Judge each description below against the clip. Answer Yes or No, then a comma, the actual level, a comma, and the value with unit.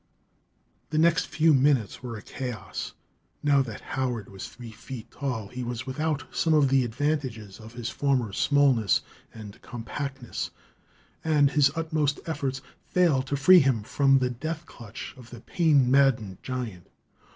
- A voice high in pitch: No, low, 130 Hz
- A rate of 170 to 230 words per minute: No, average, 150 wpm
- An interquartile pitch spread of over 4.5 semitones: No, average, 3.8 semitones